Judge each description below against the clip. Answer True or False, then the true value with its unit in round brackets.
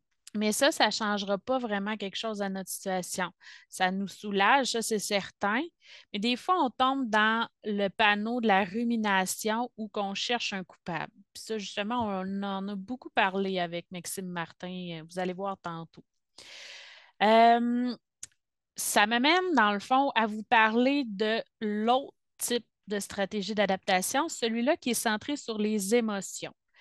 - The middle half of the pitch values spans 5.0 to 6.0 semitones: False (3.5 semitones)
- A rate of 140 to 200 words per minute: True (160 wpm)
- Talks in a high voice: True (215 Hz)